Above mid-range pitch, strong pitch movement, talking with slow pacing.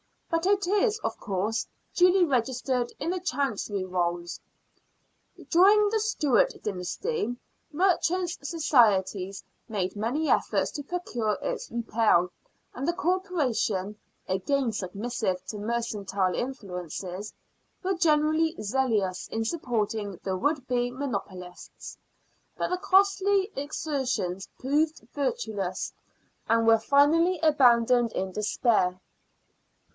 Yes: high, 245 Hz; wide, 8.0 semitones; slow, 110 wpm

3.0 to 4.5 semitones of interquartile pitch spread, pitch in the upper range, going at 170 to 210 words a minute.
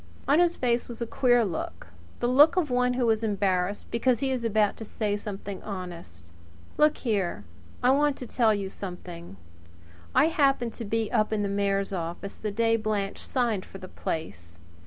Yes: average, 4.1 semitones; high, 215 Hz; average, 185 wpm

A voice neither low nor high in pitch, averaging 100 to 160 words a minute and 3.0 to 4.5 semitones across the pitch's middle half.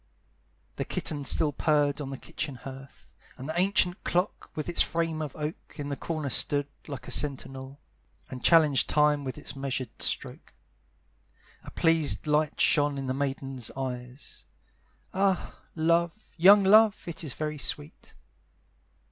Yes: medium, 150 Hz; average, 145 wpm; average, 3.4 semitones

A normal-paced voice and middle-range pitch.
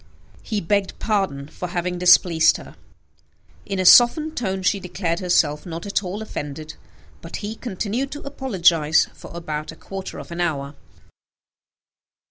Yes: average, 145 wpm; medium, 180 Hz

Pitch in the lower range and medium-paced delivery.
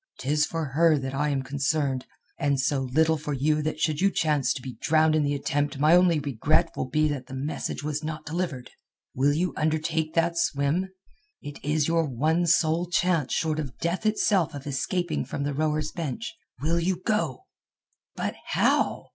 No: medium, 155 Hz; average, 185 wpm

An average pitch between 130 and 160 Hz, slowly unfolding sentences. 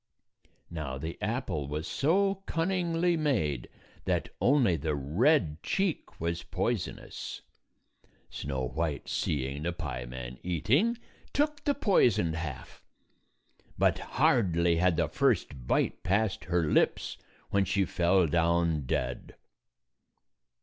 No: very low, 85 Hz; slow, 110 wpm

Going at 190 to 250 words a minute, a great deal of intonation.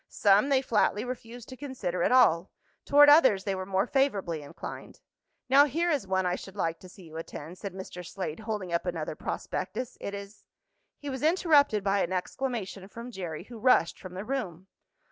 Yes: average, 195 wpm; wide, 6.0 semitones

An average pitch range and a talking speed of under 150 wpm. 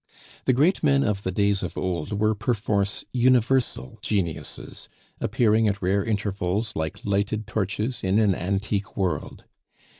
No: narrow, 2.3 semitones; average, 140 wpm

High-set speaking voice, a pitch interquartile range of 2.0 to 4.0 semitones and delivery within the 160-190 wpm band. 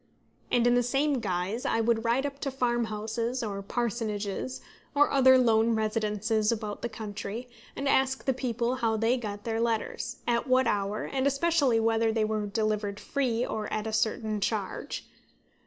Yes: high, 230 Hz; average, 2.8 semitones; average, 170 wpm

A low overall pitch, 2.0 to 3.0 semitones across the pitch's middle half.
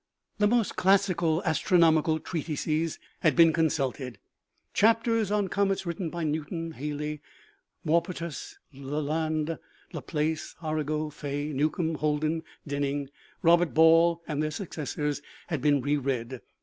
No: medium, 155 Hz; narrow, 2.4 semitones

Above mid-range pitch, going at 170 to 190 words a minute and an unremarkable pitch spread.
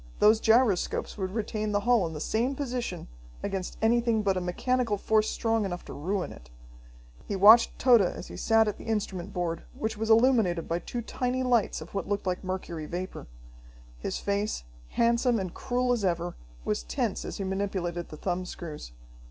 Yes: high, 205 Hz; average, 185 wpm; average, 4.4 semitones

